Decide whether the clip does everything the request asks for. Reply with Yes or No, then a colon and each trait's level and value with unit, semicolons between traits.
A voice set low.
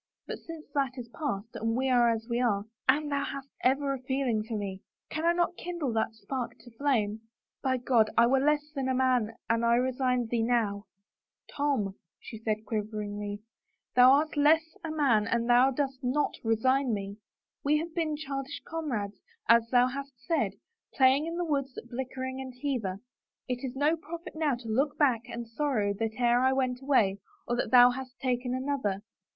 No: very high, 255 Hz